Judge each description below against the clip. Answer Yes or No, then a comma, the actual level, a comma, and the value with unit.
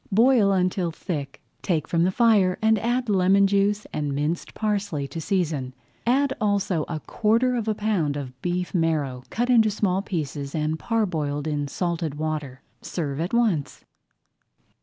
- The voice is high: No, medium, 180 Hz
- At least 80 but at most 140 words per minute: No, average, 155 wpm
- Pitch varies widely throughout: Yes, wide, 5.7 semitones